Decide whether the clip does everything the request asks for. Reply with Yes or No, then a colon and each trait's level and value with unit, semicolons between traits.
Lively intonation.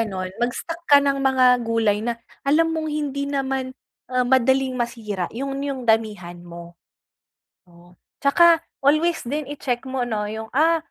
No: average, 4.1 semitones